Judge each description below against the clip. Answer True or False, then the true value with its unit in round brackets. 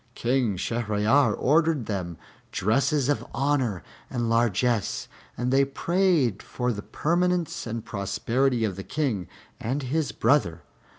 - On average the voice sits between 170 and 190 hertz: False (125 Hz)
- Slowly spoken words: True (125 wpm)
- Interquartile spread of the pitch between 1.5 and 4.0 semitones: False (5.1 semitones)